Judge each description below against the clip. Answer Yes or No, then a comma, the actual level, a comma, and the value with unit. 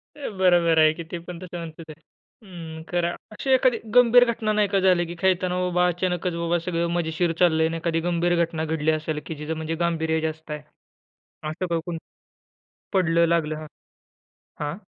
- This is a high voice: No, medium, 170 Hz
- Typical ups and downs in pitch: No, narrow, 2.1 semitones